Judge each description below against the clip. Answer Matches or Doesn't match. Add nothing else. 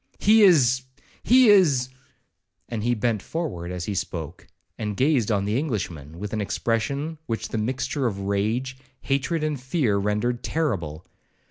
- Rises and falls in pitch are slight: Doesn't match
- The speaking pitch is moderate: Doesn't match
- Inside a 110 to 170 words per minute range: Matches